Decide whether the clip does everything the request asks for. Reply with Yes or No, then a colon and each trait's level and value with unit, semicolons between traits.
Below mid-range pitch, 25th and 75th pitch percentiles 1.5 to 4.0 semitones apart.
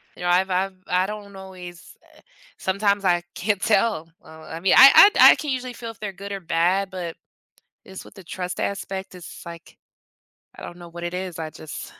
No: medium, 185 Hz; narrow, 2.4 semitones